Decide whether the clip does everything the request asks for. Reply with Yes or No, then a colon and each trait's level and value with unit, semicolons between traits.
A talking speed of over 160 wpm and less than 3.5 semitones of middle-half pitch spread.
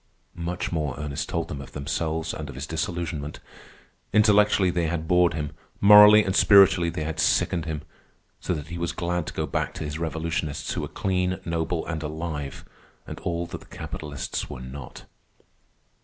Yes: average, 175 wpm; narrow, 2.5 semitones